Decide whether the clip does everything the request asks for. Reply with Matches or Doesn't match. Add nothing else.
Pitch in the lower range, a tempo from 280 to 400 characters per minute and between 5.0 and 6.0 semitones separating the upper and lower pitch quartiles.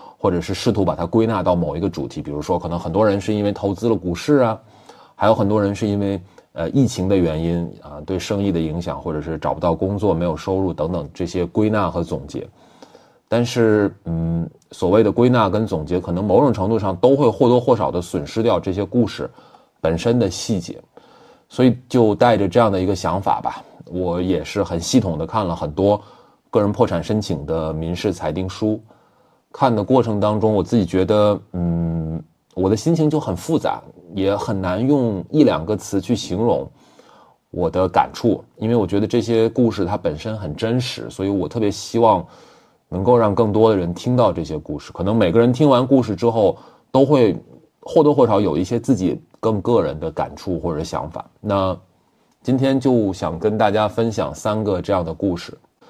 Doesn't match